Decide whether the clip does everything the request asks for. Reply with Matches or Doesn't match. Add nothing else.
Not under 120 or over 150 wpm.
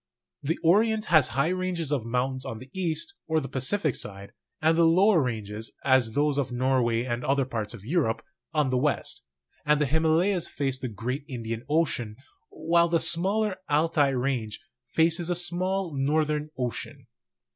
Doesn't match